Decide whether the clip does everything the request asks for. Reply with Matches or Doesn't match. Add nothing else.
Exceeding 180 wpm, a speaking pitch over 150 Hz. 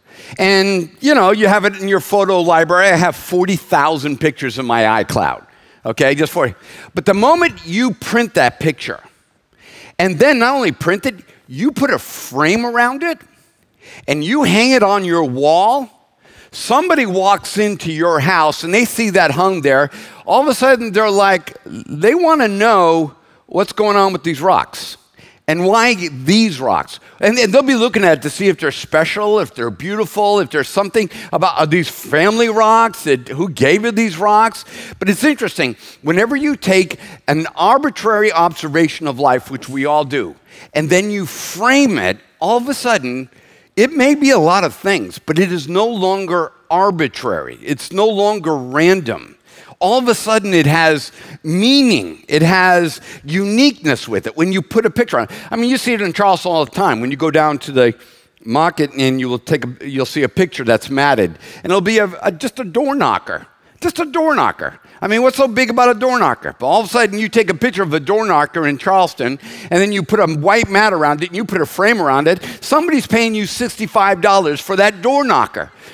Matches